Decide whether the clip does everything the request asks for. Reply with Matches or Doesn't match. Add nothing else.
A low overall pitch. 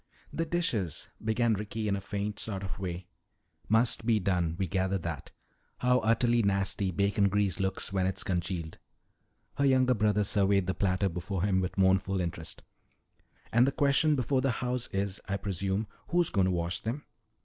Matches